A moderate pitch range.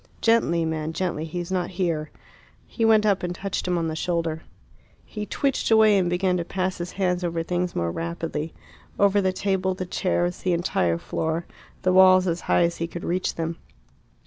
No: narrow, 2.1 semitones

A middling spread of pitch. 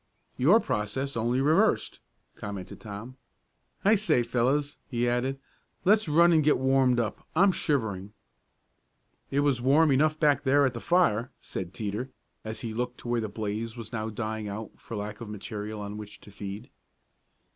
Yes: average, 5.0 semitones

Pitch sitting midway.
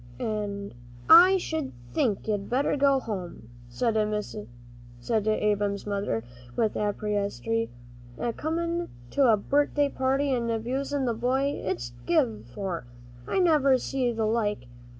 No: high, 220 Hz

